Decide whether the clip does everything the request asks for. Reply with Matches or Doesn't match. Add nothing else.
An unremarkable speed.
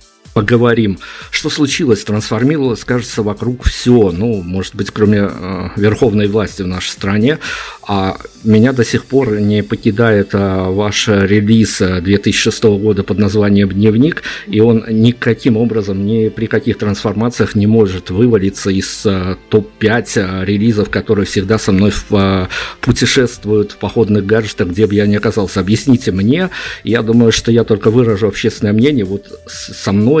Matches